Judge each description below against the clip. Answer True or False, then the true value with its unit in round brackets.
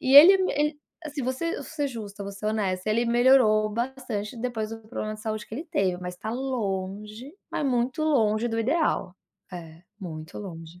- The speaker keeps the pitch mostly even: False (4.7 semitones)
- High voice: True (225 Hz)